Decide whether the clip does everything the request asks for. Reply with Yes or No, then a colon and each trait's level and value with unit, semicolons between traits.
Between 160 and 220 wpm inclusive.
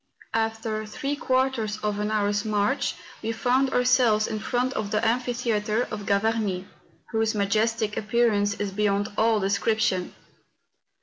No: slow, 135 wpm